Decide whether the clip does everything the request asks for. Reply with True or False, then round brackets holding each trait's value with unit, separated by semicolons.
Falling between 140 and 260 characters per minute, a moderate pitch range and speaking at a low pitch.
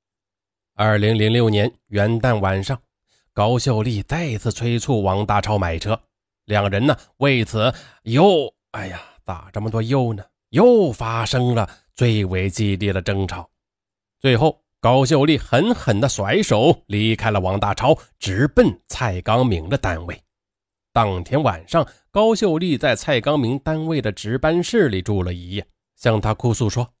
True (215 characters per minute; 4.5 semitones; 110 Hz)